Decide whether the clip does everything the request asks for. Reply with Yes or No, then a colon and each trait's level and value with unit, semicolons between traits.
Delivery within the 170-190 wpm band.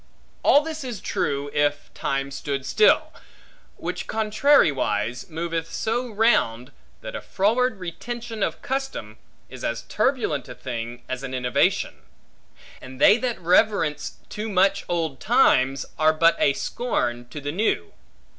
No: slow, 135 wpm